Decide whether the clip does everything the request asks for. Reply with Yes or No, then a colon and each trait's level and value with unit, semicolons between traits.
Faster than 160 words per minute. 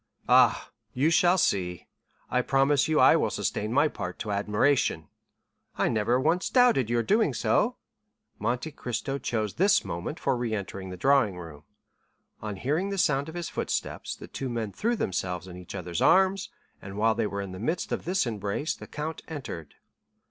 Yes: average, 180 wpm